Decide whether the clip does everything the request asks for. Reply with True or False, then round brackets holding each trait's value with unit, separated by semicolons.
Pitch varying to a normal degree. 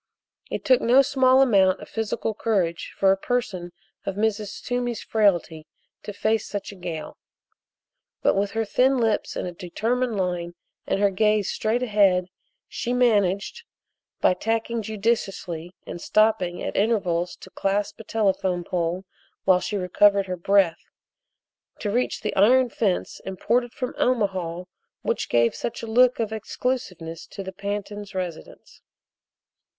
True (3.7 semitones)